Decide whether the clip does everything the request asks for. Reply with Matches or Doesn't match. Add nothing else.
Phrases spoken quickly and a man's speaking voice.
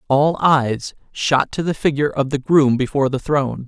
Doesn't match